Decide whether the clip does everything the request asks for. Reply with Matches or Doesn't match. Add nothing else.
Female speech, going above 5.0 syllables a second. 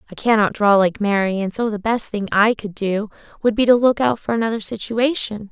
Matches